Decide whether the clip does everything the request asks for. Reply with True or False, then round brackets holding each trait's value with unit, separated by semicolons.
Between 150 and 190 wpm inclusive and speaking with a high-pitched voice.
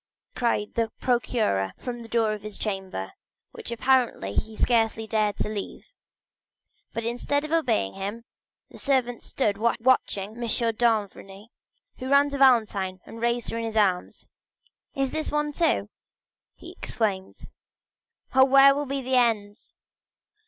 False (140 wpm; 230 Hz)